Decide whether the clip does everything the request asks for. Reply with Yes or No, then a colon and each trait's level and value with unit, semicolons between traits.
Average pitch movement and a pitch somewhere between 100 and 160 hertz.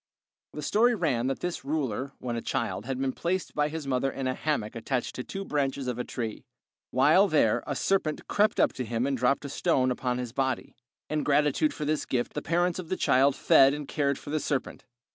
Yes: average, 3.3 semitones; medium, 140 Hz